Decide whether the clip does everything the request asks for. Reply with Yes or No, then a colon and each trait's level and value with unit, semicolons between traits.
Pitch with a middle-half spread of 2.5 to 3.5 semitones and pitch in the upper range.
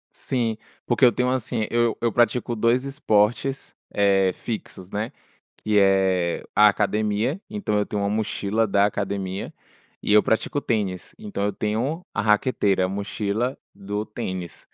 No: average, 2.9 semitones; low, 105 Hz